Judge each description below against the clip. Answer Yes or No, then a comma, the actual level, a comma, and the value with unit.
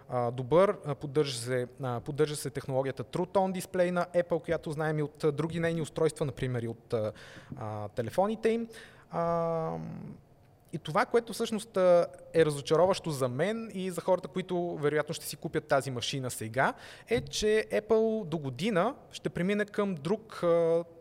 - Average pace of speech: Yes, average, 150 wpm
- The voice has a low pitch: No, medium, 165 Hz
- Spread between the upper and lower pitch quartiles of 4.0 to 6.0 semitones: Yes, average, 5.0 semitones